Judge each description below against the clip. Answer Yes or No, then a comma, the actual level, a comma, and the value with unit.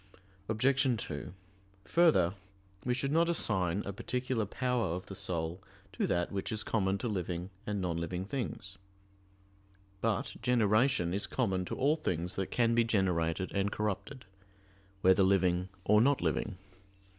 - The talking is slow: No, average, 145 wpm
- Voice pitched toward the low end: Yes, low, 100 Hz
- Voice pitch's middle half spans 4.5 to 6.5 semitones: Yes, average, 4.9 semitones